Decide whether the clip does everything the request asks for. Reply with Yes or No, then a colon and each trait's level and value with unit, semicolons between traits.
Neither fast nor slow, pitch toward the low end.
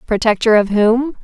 No: average, 145 wpm; high, 225 Hz